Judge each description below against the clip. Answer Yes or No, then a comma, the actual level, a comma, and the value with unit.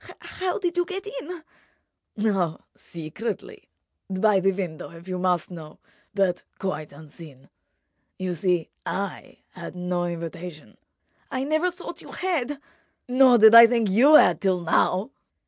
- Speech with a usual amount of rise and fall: No, wide, 7.0 semitones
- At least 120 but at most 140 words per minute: Yes, slow, 135 wpm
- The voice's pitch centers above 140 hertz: Yes, high, 190 Hz